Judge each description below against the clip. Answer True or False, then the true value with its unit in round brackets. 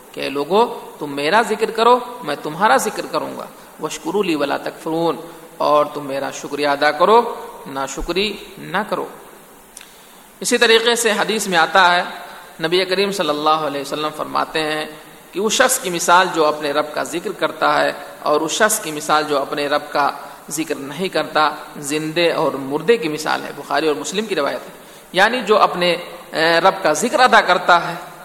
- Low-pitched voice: False (160 Hz)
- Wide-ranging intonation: False (4.9 semitones)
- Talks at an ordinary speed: True (180 wpm)